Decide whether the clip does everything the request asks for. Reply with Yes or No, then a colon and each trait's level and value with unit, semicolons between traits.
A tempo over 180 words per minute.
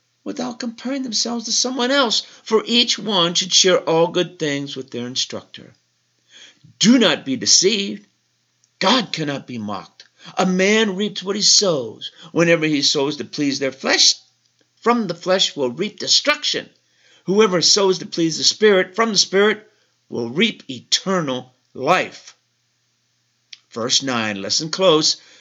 No: average, 145 wpm